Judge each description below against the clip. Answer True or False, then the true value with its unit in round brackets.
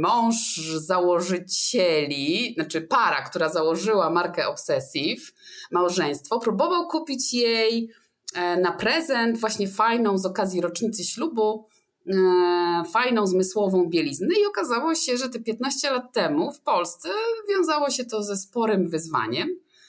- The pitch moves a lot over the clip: True (7.2 semitones)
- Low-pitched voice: False (220 Hz)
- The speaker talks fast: False (120 wpm)